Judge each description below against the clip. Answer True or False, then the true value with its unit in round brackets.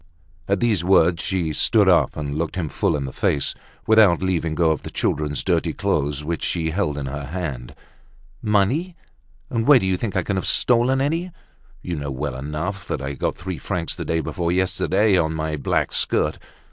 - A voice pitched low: True (85 Hz)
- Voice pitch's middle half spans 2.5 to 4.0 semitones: False (4.8 semitones)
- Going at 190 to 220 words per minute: True (195 wpm)